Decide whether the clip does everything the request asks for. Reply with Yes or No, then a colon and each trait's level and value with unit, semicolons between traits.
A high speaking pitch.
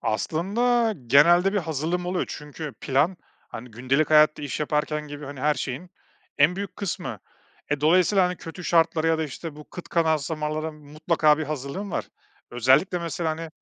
No: medium, 155 Hz